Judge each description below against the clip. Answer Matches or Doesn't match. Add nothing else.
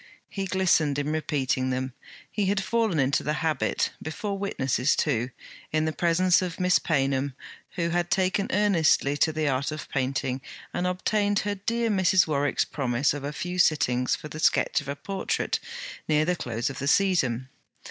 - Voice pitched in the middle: Matches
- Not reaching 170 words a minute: Doesn't match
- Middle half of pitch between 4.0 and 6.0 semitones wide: Matches